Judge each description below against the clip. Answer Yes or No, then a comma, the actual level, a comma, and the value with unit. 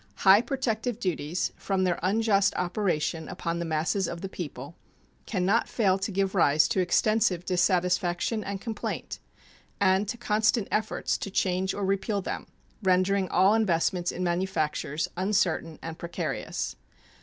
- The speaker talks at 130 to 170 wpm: Yes, average, 145 wpm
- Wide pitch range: No, average, 2.8 semitones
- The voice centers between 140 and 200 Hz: Yes, high, 190 Hz